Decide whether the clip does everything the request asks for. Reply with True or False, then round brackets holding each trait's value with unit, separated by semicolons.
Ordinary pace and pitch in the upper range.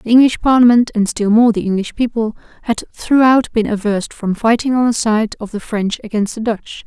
False (210 wpm; 225 Hz)